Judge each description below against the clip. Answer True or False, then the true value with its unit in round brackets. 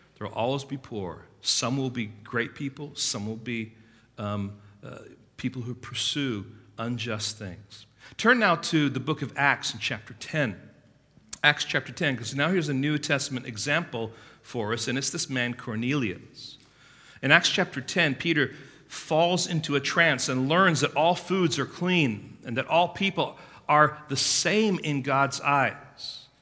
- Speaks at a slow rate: False (165 wpm)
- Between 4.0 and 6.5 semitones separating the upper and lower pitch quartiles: True (4.3 semitones)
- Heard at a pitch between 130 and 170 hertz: True (135 Hz)